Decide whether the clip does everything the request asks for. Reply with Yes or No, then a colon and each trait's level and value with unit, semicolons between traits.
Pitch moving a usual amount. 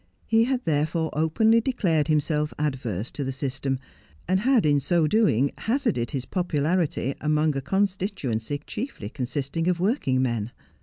No: wide, 5.7 semitones